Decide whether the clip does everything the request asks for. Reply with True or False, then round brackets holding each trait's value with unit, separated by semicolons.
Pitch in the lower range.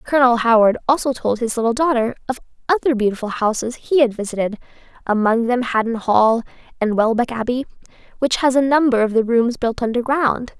False (240 Hz)